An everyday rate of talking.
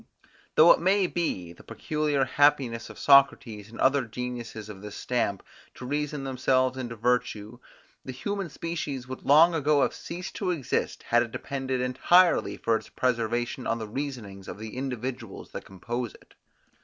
Yes: average, 165 wpm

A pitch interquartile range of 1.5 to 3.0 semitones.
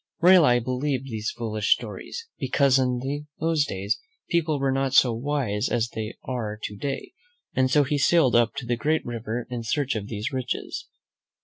No: average, 3.8 semitones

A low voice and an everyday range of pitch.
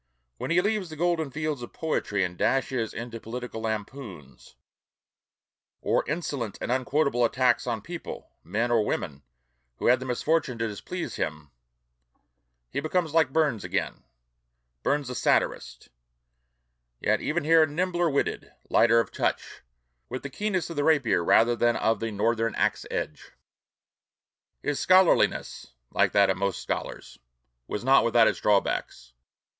No: low, 125 Hz; wide, 5.8 semitones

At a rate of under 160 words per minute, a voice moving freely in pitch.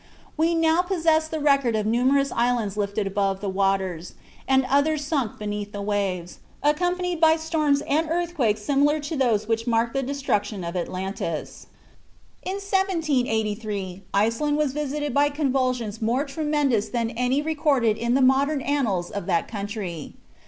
Yes: average, 150 wpm; wide, 6.2 semitones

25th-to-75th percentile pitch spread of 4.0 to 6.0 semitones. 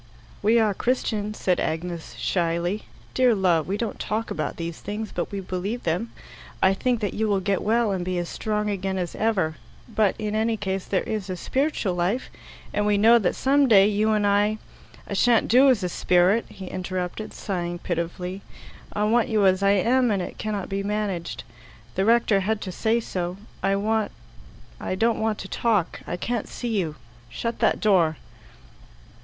No: average, 3.1 semitones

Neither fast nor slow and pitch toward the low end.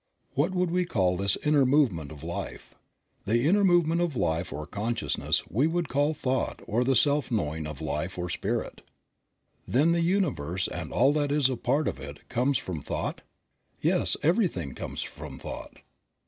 Yes: average, 175 wpm; low, 125 Hz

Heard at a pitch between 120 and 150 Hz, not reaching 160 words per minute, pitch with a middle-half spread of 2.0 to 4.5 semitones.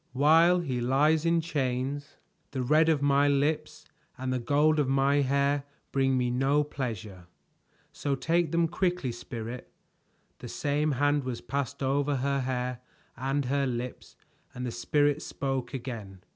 Yes: medium, 140 Hz; average, 150 wpm; narrow, 2.6 semitones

